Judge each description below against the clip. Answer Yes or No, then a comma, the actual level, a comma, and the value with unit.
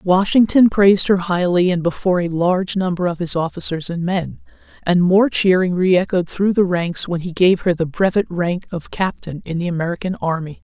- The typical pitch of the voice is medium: Yes, medium, 180 Hz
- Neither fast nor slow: Yes, average, 190 wpm